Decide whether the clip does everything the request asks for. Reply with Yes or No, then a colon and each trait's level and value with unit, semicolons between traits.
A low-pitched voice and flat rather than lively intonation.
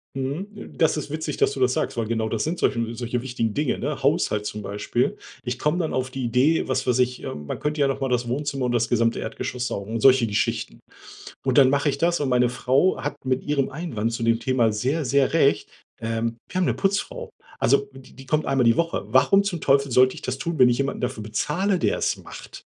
No: low, 130 Hz; average, 3.7 semitones